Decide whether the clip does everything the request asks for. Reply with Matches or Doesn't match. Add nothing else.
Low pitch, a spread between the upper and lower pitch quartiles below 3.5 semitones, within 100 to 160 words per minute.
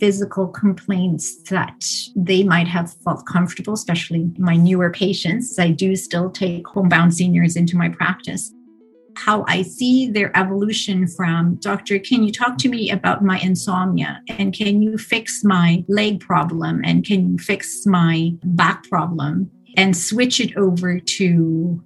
Doesn't match